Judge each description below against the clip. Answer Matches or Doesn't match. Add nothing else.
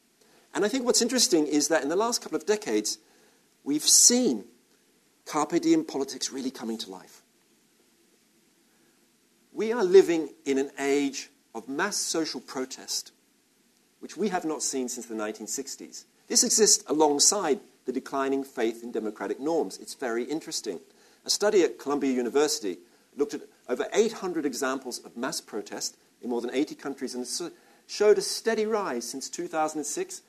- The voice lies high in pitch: Doesn't match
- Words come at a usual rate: Matches